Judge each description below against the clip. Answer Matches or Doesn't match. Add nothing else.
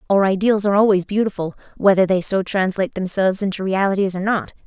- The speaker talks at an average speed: Matches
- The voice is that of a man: Doesn't match